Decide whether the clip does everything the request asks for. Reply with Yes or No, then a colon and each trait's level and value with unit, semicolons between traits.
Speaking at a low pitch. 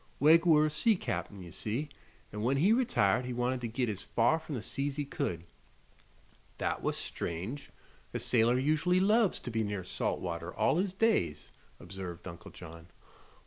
Yes: low, 125 Hz